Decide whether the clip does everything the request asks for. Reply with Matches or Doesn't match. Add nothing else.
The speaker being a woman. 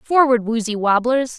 Matches